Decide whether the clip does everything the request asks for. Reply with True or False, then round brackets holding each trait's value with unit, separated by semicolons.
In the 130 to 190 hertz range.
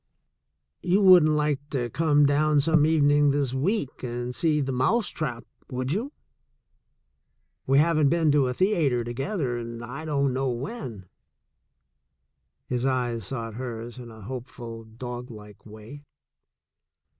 True (135 Hz)